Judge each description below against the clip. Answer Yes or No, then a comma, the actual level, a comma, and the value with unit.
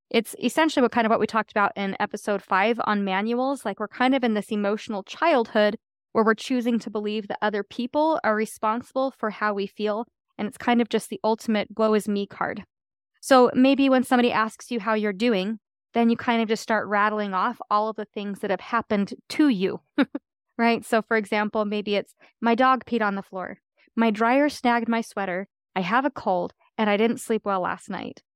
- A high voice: Yes, high, 220 Hz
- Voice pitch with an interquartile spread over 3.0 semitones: No, narrow, 2.5 semitones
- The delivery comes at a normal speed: No, fast, 215 wpm